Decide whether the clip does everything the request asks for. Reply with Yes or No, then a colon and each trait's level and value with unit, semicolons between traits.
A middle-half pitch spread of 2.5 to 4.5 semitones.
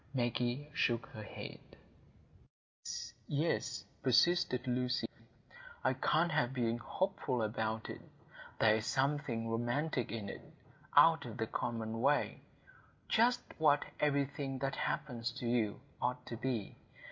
Yes: average, 3.9 semitones